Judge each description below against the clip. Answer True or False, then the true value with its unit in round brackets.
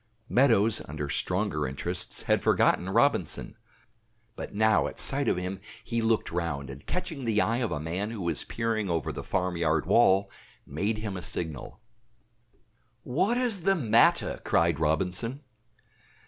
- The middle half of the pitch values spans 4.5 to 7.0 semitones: True (5.5 semitones)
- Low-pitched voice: True (100 Hz)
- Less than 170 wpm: True (145 wpm)